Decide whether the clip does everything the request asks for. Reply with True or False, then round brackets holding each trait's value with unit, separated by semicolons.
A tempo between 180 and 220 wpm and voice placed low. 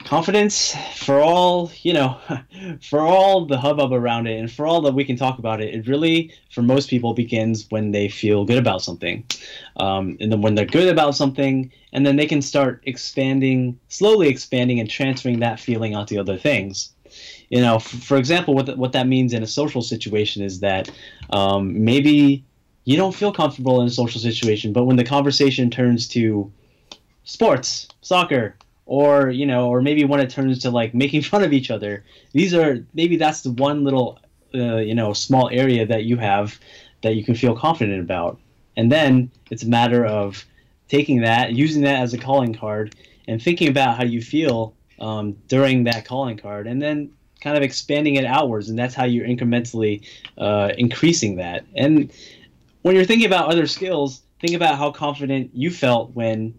True (190 wpm; 125 Hz)